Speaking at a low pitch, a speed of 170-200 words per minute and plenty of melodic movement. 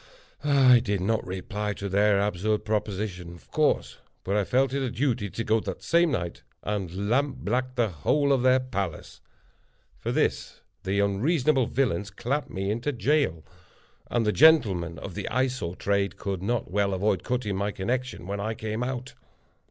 No: low, 105 Hz; average, 175 wpm; average, 4.5 semitones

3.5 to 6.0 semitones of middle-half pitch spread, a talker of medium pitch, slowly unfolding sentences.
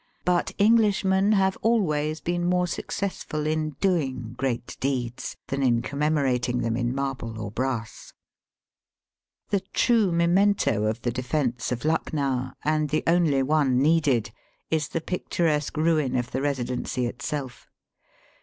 Yes: average, 5.2 semitones; medium, 145 Hz; slow, 130 wpm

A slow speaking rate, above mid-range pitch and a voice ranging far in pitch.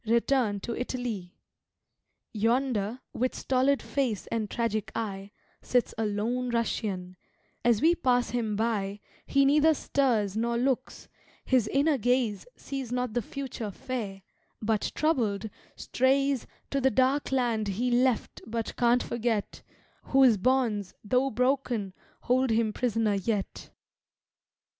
No: slow, 125 wpm; high, 235 Hz; average, 3.4 semitones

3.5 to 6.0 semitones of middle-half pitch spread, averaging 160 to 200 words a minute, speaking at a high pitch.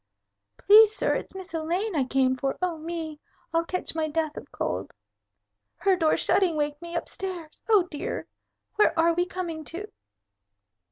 No: average, 3.0 semitones; average, 165 wpm; very high, 335 Hz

